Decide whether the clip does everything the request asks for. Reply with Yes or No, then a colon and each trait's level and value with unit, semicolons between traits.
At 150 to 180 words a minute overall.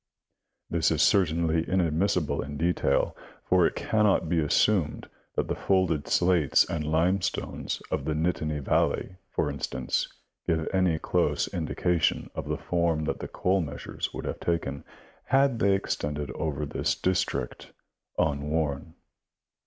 No: slow, 135 wpm